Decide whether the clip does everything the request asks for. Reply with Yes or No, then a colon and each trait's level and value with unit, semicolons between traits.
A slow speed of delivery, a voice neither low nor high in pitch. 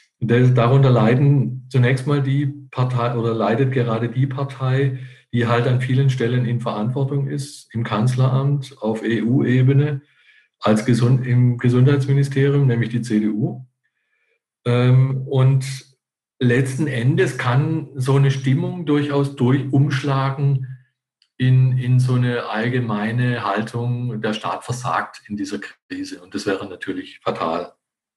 No: slow, 120 wpm; low, 130 Hz